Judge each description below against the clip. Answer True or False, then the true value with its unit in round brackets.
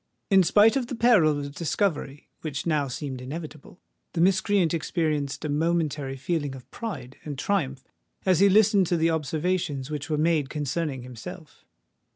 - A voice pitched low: False (155 Hz)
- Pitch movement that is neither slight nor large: True (4.4 semitones)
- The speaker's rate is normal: True (160 wpm)